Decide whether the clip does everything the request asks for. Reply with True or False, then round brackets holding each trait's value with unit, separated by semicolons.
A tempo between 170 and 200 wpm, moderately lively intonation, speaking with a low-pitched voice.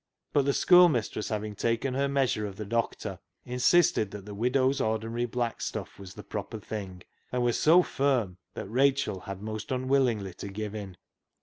True (180 wpm; 4.2 semitones; 115 Hz)